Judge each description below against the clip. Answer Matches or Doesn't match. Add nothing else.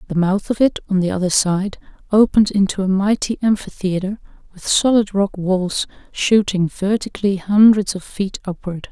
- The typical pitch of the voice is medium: Doesn't match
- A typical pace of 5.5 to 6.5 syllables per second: Doesn't match